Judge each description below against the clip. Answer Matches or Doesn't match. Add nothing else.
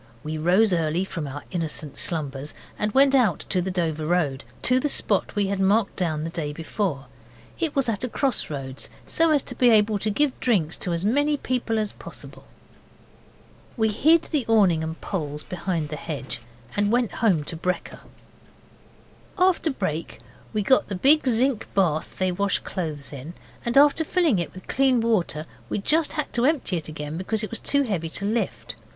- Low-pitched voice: Doesn't match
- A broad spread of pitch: Matches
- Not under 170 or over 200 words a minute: Matches